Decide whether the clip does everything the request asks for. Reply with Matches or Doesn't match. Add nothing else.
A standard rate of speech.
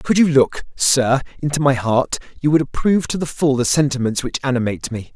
Doesn't match